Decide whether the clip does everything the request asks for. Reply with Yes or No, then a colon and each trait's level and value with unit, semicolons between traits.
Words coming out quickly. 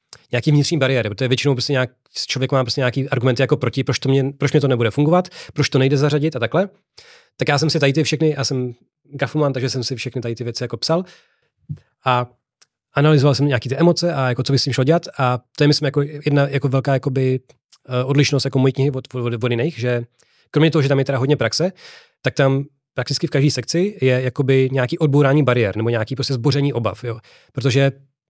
Yes: fast, 225 wpm